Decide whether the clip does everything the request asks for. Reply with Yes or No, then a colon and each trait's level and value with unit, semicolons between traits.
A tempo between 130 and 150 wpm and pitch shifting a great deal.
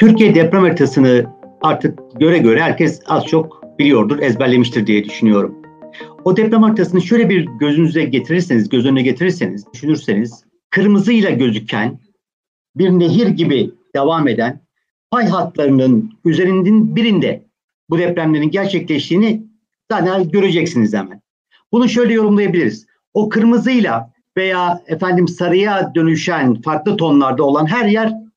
No: average, 115 wpm; wide, 6.6 semitones